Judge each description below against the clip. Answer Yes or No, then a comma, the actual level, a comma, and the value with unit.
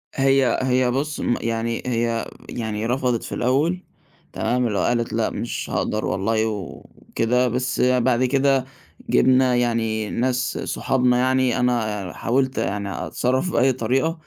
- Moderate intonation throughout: No, narrow, 2.3 semitones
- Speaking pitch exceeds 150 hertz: No, low, 125 Hz